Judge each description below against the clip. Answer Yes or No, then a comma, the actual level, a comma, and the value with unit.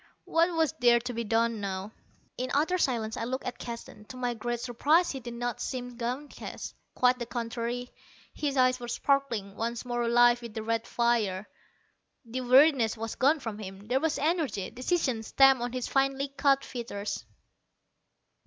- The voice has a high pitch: Yes, high, 240 Hz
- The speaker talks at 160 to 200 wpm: Yes, average, 170 wpm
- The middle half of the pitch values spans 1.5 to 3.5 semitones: Yes, average, 2.7 semitones